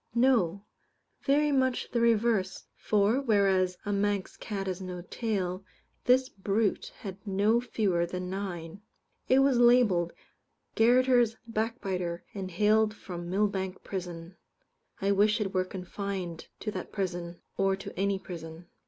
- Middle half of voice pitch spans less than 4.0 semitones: Yes, average, 3.4 semitones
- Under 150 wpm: Yes, slow, 135 wpm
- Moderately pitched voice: No, high, 200 Hz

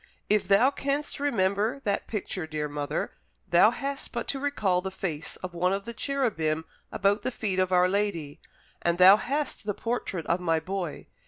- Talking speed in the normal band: Yes, average, 180 wpm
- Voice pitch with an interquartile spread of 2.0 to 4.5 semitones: No, average, 5.3 semitones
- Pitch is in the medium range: No, high, 195 Hz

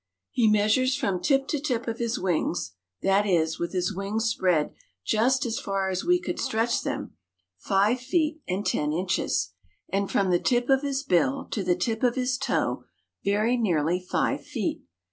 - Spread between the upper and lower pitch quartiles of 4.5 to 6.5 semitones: Yes, wide, 5.5 semitones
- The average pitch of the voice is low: No, high, 215 Hz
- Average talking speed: Yes, average, 180 wpm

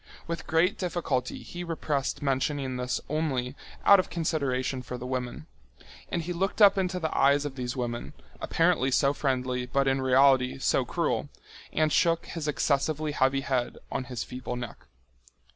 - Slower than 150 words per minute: No, average, 160 wpm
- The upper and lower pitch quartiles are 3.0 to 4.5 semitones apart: Yes, average, 4.0 semitones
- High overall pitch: No, medium, 140 Hz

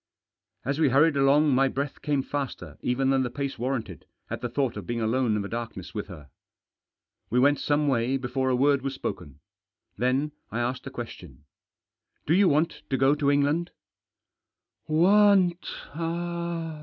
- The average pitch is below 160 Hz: Yes, low, 135 Hz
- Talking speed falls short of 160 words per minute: No, average, 175 wpm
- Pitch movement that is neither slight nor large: Yes, average, 3.6 semitones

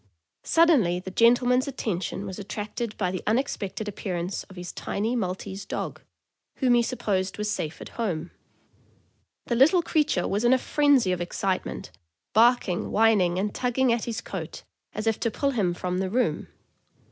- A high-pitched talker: Yes, high, 210 Hz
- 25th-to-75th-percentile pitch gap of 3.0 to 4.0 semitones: No, average, 4.7 semitones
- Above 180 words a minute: No, average, 160 wpm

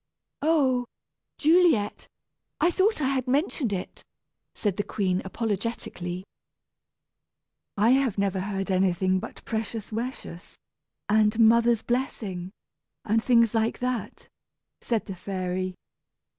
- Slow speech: Yes, slow, 110 wpm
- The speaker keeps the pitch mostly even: No, average, 4.6 semitones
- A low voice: No, high, 220 Hz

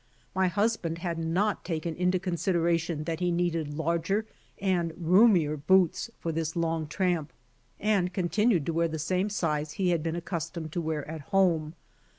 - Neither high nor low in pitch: Yes, medium, 170 Hz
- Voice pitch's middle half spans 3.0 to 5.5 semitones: No, narrow, 2.4 semitones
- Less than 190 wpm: Yes, average, 160 wpm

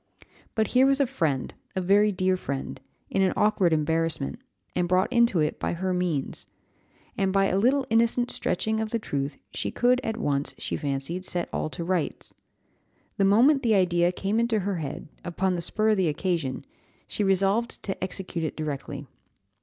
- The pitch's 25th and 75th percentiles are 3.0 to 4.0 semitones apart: No, average, 4.7 semitones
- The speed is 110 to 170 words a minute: No, average, 180 wpm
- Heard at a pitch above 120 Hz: Yes, high, 190 Hz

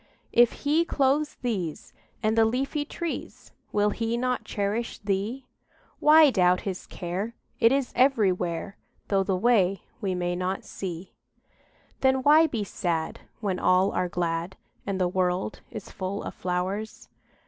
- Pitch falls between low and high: No, high, 200 Hz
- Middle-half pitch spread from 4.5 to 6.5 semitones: Yes, average, 5.2 semitones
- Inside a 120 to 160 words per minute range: Yes, average, 145 wpm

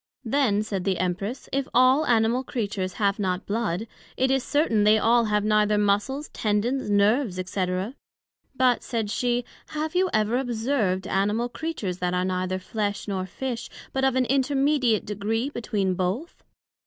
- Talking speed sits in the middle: Yes, average, 155 wpm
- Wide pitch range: No, average, 4.5 semitones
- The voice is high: Yes, high, 220 Hz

